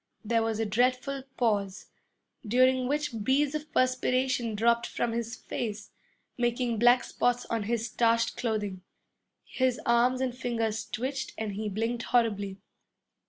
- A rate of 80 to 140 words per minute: Yes, slow, 135 wpm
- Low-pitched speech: No, high, 235 Hz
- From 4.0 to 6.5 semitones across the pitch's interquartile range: No, narrow, 2.5 semitones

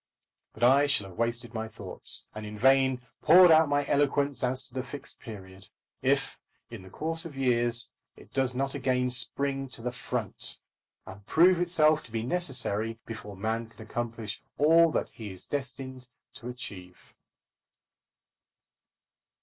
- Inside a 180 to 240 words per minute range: No, average, 155 wpm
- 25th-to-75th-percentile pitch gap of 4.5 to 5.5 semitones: No, average, 4.0 semitones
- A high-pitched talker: No, low, 125 Hz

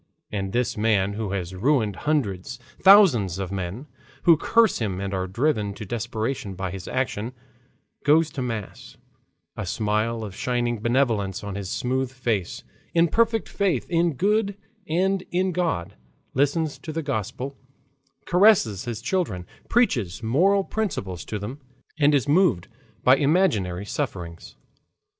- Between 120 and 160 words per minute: Yes, average, 140 wpm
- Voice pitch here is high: No, low, 120 Hz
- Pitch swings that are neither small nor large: No, wide, 8.0 semitones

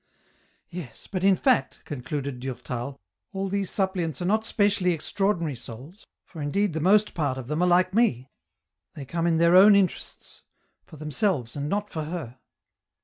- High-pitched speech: No, medium, 170 Hz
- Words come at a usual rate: Yes, average, 180 wpm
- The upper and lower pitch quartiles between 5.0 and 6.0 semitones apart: Yes, wide, 5.6 semitones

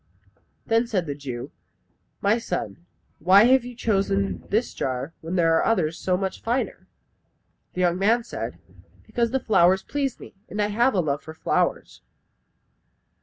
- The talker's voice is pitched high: Yes, high, 195 Hz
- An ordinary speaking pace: Yes, average, 160 wpm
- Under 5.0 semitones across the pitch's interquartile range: No, wide, 5.5 semitones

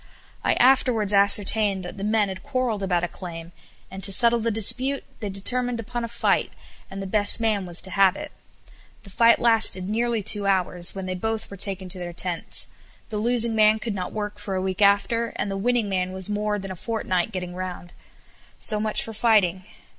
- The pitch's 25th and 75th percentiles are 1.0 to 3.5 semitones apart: Yes, average, 3.1 semitones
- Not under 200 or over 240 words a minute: Yes, fast, 205 wpm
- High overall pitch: Yes, high, 205 Hz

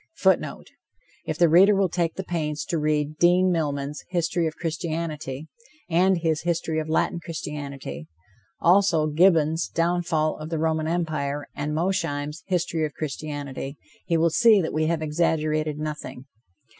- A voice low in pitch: No, medium, 160 Hz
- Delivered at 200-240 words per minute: No, average, 145 wpm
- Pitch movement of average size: No, narrow, 2.1 semitones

